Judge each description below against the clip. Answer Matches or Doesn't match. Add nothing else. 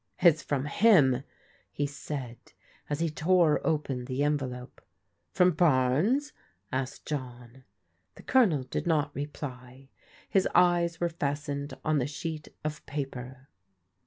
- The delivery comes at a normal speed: Doesn't match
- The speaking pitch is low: Doesn't match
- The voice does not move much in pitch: Doesn't match